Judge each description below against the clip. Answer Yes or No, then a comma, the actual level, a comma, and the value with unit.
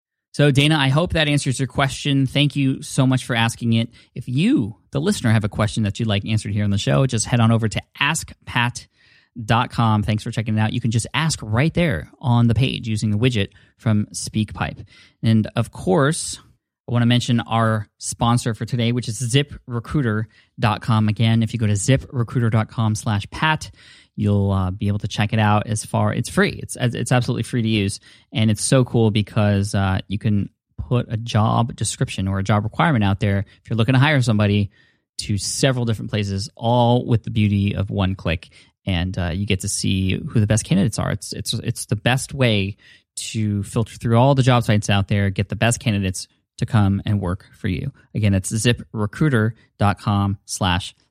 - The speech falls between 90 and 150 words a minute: No, average, 195 wpm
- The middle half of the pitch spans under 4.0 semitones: Yes, average, 3.0 semitones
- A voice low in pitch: Yes, low, 115 Hz